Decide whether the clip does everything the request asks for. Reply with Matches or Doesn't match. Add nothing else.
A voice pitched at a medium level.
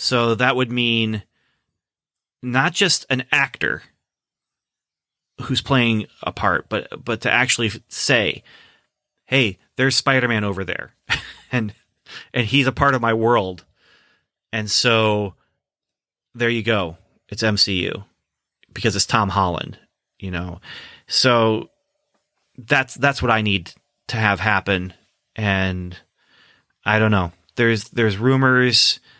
Doesn't match